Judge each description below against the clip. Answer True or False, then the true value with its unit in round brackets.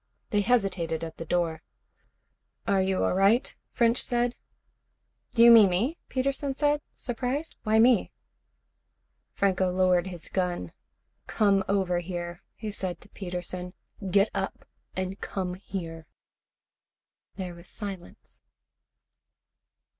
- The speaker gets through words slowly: True (115 wpm)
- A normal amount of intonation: True (4.3 semitones)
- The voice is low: False (190 Hz)